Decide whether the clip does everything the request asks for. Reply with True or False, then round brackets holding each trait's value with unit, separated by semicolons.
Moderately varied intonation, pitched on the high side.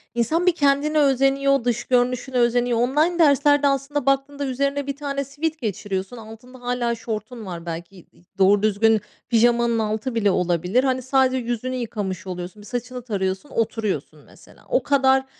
True (4.2 semitones; 245 Hz)